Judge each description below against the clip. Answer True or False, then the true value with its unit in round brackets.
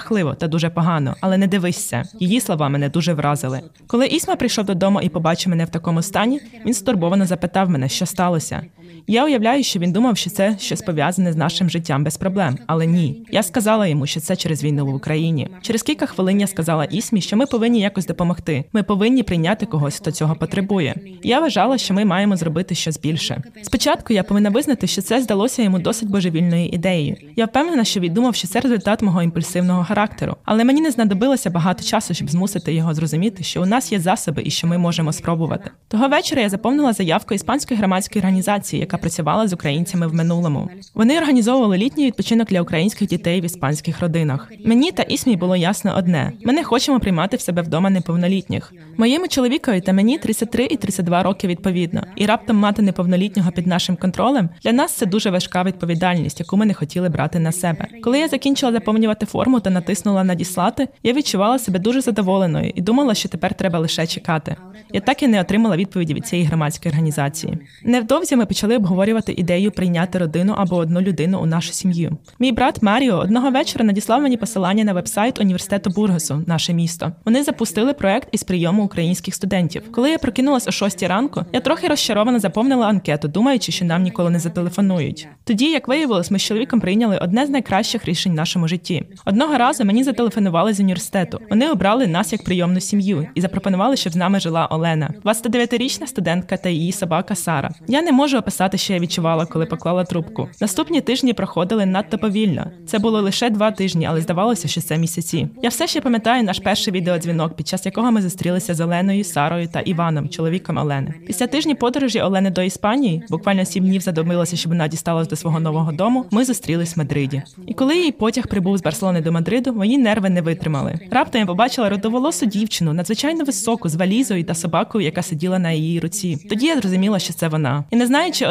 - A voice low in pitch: False (190 Hz)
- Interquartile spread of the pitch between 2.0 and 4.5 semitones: False (5.0 semitones)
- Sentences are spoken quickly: True (190 wpm)